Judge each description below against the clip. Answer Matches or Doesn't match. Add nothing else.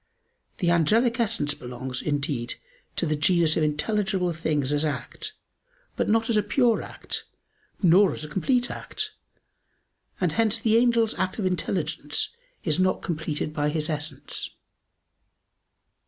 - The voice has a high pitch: Doesn't match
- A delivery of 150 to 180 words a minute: Doesn't match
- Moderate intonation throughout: Doesn't match